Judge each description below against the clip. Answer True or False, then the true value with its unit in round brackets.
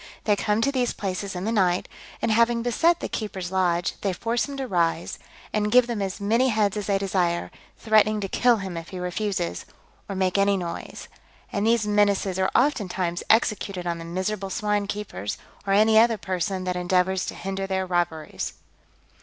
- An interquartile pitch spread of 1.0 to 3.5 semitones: True (2.9 semitones)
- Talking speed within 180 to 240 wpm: True (185 wpm)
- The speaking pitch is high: True (195 Hz)